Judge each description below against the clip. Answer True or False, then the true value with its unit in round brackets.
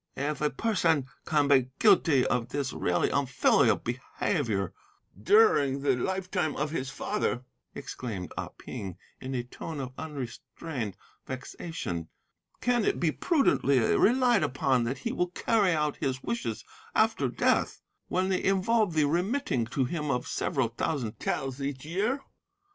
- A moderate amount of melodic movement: False (6.2 semitones)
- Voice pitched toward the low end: False (145 Hz)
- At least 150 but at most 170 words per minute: False (140 wpm)